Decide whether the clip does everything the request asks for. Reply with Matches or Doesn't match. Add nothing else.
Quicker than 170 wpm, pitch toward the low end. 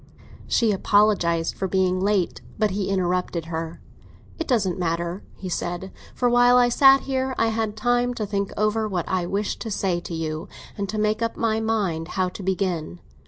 Doesn't match